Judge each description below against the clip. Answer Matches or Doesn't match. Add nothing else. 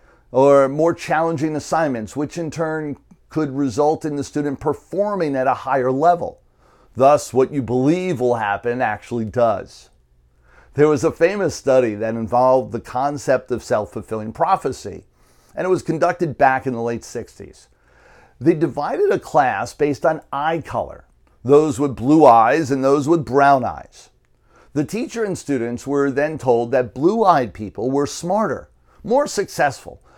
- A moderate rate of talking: Matches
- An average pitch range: Matches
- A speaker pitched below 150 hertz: Matches